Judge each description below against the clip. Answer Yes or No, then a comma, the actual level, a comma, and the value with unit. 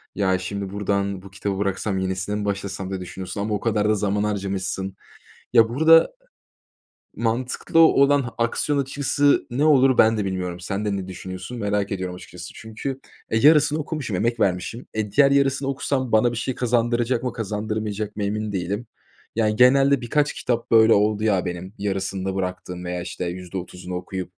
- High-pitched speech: No, low, 105 Hz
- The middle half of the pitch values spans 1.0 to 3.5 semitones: No, average, 4.2 semitones